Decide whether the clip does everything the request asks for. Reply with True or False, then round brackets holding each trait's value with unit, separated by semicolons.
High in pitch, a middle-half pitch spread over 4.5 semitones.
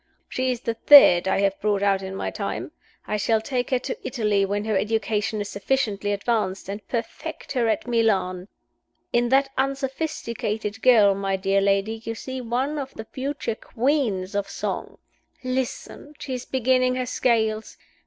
False (225 Hz; 4.2 semitones)